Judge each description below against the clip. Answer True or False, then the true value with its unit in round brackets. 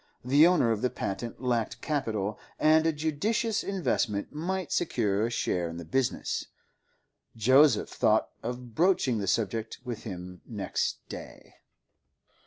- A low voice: True (125 Hz)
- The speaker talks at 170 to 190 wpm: False (135 wpm)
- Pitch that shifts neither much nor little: False (6.4 semitones)